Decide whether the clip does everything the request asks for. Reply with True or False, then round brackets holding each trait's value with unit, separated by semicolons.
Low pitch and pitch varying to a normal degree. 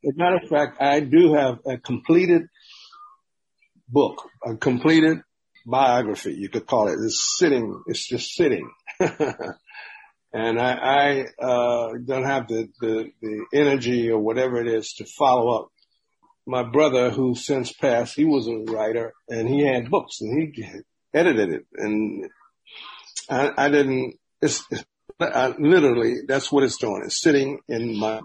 True (130 Hz; 4.5 semitones)